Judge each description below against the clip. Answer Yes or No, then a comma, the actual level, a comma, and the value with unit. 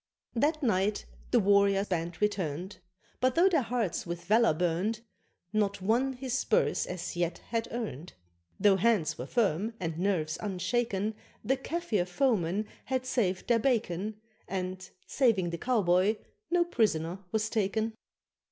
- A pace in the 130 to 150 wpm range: Yes, average, 140 wpm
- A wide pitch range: No, average, 4.7 semitones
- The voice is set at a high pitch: Yes, high, 205 Hz